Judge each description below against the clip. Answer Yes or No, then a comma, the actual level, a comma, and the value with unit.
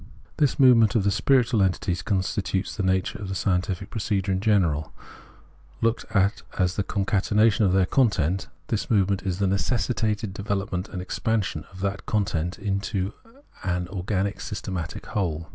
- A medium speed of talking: Yes, average, 155 wpm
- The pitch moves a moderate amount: No, narrow, 2.3 semitones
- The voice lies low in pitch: Yes, low, 100 Hz